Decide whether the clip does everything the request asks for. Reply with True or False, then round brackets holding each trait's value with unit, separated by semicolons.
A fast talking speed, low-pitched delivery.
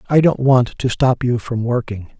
True (220 wpm; 125 Hz)